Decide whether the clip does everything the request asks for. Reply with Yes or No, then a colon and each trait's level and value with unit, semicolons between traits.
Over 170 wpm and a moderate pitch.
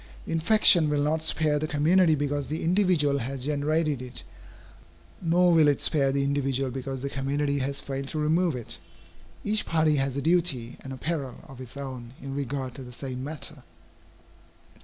Yes: average, 180 wpm; medium, 145 Hz